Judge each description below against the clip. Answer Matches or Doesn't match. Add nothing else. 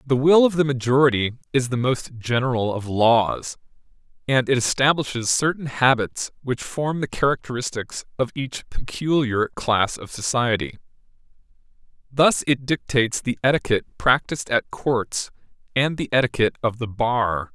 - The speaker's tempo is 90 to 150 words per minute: Matches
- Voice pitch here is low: Matches